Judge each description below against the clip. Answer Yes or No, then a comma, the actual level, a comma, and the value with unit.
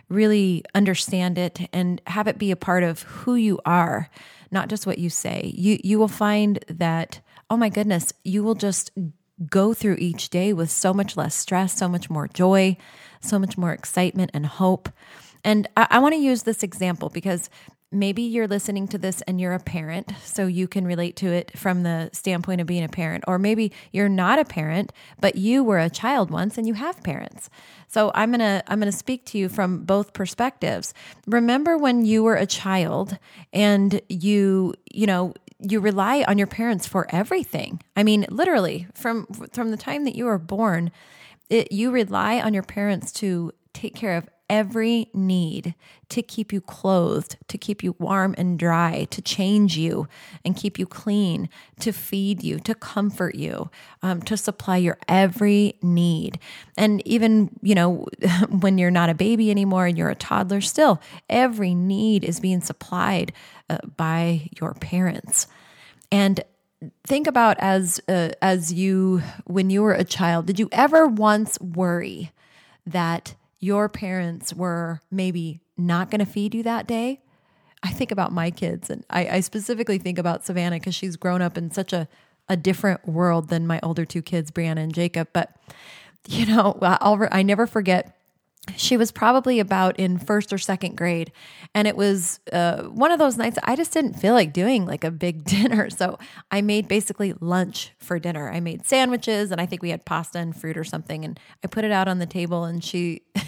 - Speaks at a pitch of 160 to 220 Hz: Yes, high, 190 Hz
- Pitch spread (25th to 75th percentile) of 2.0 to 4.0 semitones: Yes, average, 3.3 semitones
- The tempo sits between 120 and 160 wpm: No, average, 185 wpm